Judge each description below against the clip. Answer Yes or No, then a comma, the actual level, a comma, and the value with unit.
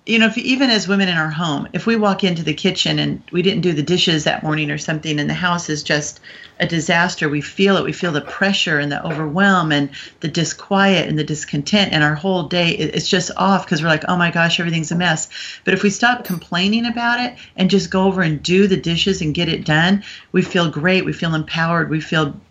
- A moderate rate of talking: No, fast, 245 wpm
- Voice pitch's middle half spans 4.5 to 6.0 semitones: No, average, 3.7 semitones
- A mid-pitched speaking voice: Yes, medium, 175 Hz